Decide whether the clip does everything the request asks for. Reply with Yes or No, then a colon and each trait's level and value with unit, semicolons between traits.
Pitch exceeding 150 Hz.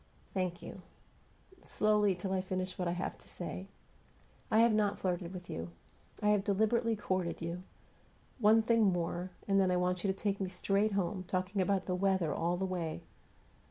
Yes: high, 190 Hz